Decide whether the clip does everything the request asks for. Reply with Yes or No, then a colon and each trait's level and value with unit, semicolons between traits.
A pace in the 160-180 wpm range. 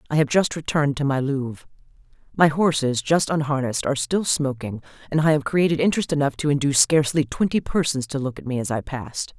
No: fast, 205 wpm